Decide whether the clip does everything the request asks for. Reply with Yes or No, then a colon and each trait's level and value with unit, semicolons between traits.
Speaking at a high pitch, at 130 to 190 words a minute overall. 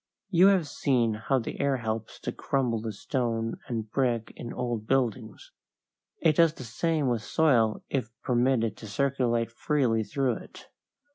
No: low, 120 Hz; average, 155 wpm